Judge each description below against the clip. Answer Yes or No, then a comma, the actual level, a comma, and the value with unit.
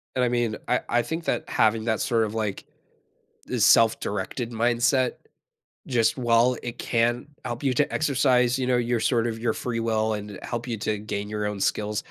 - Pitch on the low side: Yes, low, 115 Hz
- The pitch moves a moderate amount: No, narrow, 2.0 semitones